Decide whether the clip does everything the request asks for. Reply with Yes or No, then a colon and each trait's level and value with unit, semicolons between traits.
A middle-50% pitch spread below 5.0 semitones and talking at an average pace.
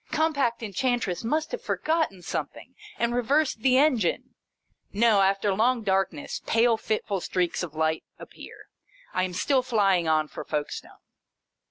No: wide, 5.5 semitones; average, 150 wpm